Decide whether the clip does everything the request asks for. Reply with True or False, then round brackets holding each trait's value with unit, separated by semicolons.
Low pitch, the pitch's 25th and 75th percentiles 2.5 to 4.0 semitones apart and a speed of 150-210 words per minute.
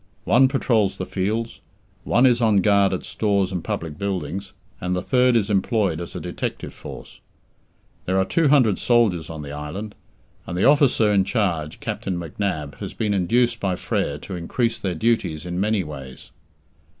False (100 Hz; 4.6 semitones; 175 wpm)